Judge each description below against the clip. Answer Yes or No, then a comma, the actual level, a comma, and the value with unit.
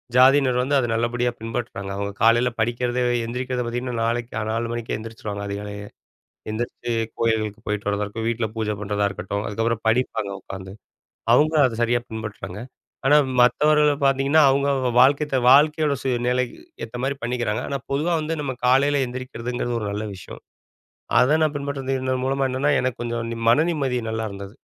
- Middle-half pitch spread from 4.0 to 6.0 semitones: No, average, 3.3 semitones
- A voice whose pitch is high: No, low, 120 Hz